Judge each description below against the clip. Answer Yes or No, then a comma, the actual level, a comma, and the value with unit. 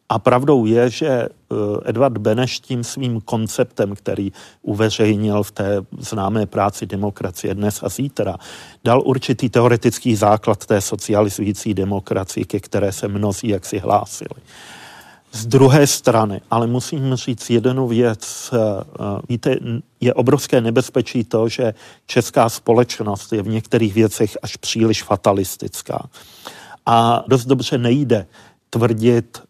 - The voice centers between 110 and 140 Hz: Yes, low, 115 Hz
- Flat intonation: No, average, 3.1 semitones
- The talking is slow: No, average, 125 wpm